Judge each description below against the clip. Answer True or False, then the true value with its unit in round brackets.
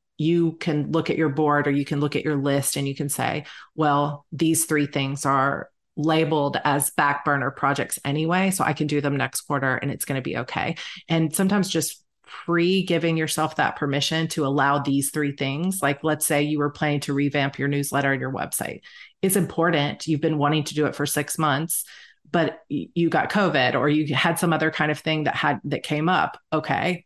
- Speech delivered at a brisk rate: True (215 wpm)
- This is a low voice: False (150 Hz)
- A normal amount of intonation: False (2.2 semitones)